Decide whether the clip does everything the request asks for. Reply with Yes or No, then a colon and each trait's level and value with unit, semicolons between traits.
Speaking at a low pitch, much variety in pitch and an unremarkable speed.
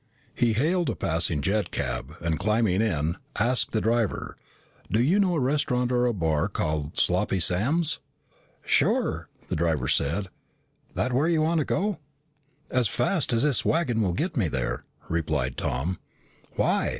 Yes: low, 110 Hz; wide, 8.9 semitones; average, 160 wpm